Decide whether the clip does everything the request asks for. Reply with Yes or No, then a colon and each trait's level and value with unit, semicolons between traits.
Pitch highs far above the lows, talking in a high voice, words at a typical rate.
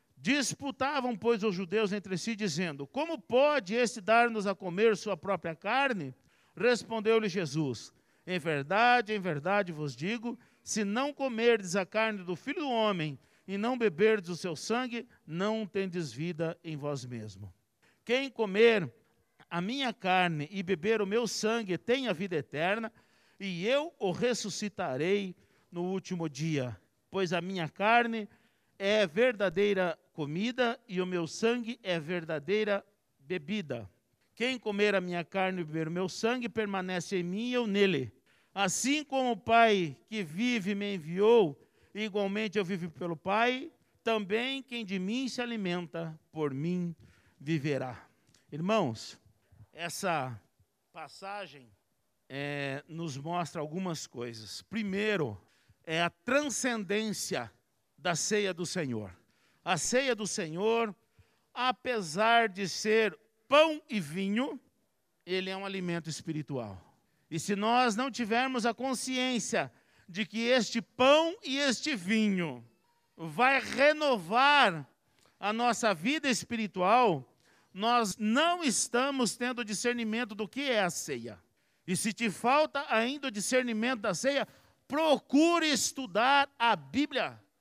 Yes: wide, 5.9 semitones; high, 205 Hz; average, 130 wpm